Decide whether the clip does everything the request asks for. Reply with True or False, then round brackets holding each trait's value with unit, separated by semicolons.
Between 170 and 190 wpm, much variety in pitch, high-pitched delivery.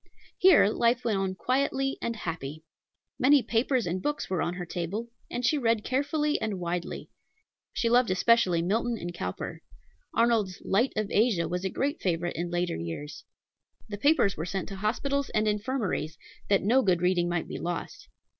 True (175 wpm; 5.7 semitones; 205 Hz)